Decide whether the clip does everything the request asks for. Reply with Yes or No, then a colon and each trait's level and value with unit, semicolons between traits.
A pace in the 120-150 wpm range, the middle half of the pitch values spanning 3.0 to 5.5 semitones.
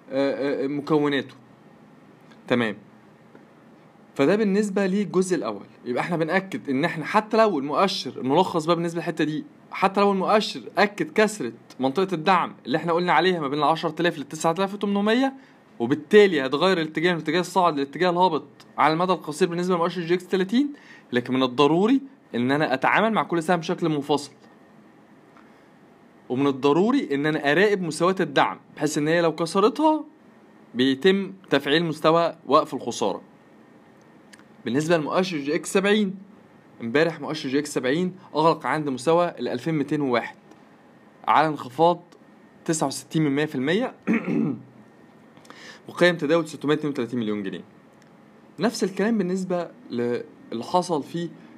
Yes: average, 125 wpm; average, 4.7 semitones